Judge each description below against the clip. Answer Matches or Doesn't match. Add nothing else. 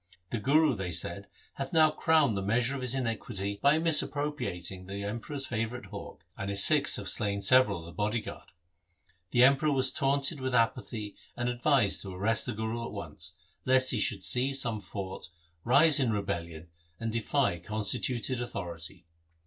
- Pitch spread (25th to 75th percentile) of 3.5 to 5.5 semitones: Matches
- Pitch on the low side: Matches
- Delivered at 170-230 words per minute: Matches